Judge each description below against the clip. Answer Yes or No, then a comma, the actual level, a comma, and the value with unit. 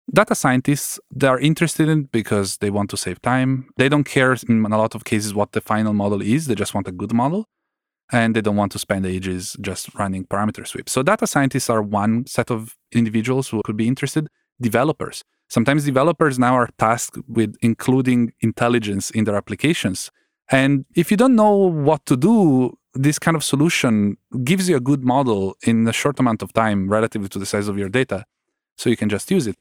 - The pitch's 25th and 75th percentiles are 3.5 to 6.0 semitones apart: Yes, average, 5.1 semitones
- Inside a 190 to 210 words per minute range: Yes, fast, 205 wpm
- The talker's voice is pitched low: Yes, low, 120 Hz